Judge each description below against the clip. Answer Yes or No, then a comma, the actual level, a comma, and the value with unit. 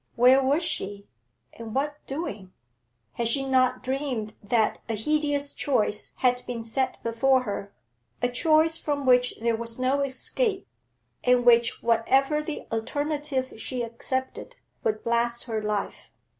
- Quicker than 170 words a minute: No, average, 140 wpm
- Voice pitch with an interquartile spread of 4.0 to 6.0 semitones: No, average, 3.6 semitones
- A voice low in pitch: No, very high, 255 Hz